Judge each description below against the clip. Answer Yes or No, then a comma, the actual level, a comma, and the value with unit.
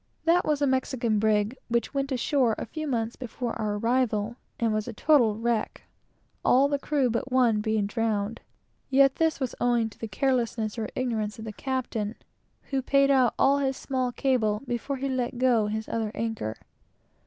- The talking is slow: No, average, 175 wpm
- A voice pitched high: Yes, high, 240 Hz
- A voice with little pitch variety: No, average, 3.4 semitones